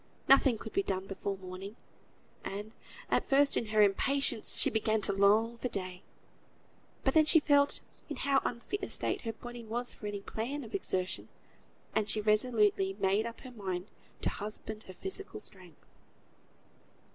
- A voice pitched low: No, high, 215 Hz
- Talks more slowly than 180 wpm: Yes, average, 165 wpm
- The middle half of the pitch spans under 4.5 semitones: Yes, average, 4.1 semitones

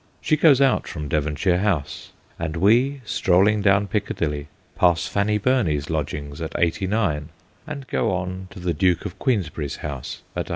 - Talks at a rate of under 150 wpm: No, average, 160 wpm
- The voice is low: Yes, very low, 90 Hz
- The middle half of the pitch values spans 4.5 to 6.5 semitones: Yes, wide, 5.5 semitones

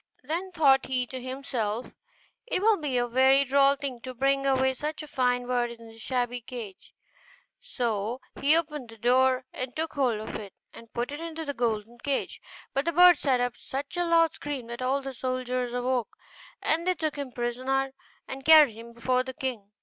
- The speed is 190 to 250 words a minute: Yes, average, 195 wpm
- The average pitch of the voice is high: Yes, very high, 260 Hz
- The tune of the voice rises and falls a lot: No, average, 2.8 semitones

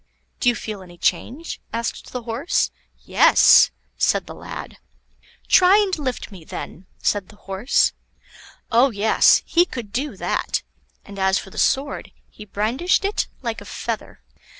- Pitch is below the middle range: No, high, 230 Hz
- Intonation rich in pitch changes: Yes, wide, 5.7 semitones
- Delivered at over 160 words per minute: No, average, 150 wpm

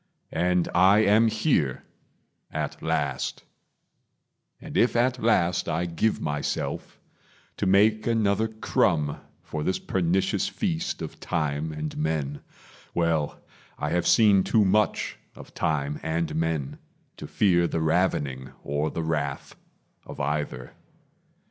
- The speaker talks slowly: Yes, slow, 125 wpm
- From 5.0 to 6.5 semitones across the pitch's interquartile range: Yes, wide, 5.5 semitones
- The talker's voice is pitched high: No, very low, 85 Hz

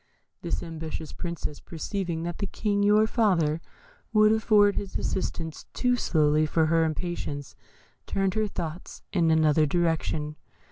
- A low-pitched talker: No, medium, 170 Hz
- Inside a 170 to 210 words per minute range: No, slow, 135 wpm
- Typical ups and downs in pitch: Yes, average, 4.3 semitones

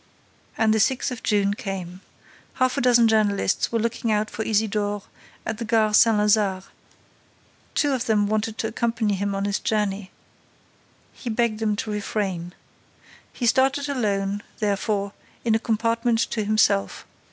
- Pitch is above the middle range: Yes, high, 215 Hz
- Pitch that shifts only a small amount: Yes, narrow, 2.1 semitones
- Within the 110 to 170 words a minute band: Yes, average, 150 wpm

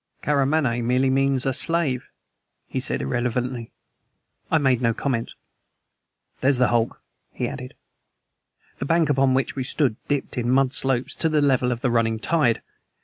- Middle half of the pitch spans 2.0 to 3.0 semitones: Yes, narrow, 2.5 semitones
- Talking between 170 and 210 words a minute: No, average, 155 wpm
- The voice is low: Yes, low, 130 Hz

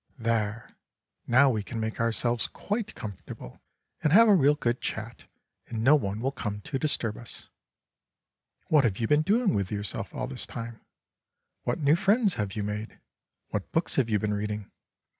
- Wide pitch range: Yes, wide, 5.8 semitones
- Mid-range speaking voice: No, low, 115 Hz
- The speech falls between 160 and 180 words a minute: Yes, average, 175 wpm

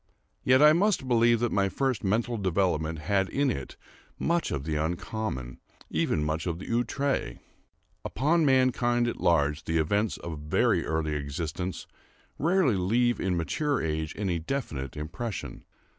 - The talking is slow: No, average, 145 wpm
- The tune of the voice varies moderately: No, wide, 7.7 semitones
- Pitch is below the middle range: Yes, very low, 95 Hz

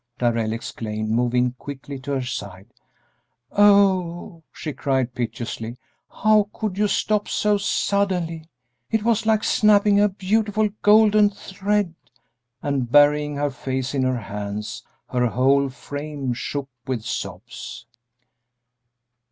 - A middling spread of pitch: No, wide, 8.6 semitones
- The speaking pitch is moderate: Yes, medium, 145 Hz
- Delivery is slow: Yes, slow, 120 wpm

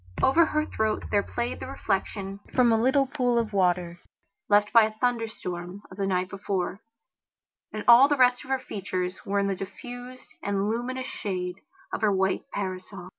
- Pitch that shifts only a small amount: No, average, 4.4 semitones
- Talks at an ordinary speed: Yes, average, 180 wpm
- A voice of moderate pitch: No, high, 210 Hz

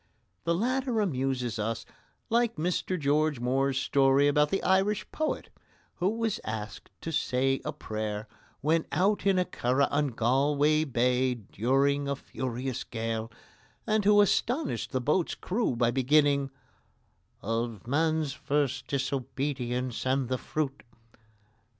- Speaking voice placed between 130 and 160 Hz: Yes, medium, 140 Hz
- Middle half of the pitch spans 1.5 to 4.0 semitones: No, average, 4.7 semitones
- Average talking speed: No, slow, 130 wpm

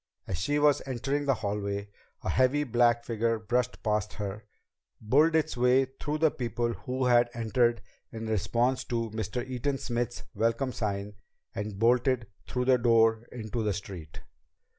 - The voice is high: No, low, 120 Hz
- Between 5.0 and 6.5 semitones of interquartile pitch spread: No, average, 2.8 semitones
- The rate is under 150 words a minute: No, average, 155 wpm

